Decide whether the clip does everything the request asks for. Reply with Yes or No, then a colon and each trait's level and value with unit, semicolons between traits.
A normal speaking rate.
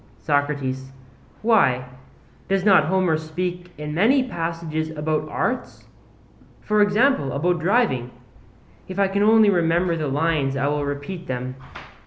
No: slow, 130 wpm